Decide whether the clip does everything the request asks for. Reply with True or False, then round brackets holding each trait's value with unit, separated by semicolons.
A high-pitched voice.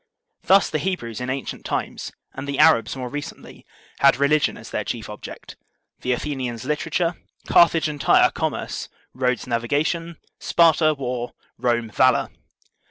False (135 Hz)